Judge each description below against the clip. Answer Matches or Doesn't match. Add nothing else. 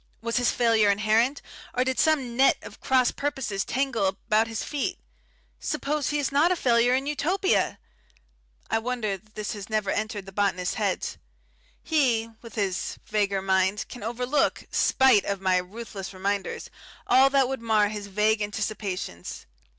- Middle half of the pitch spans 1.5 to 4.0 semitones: Doesn't match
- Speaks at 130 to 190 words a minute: Matches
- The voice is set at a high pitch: Matches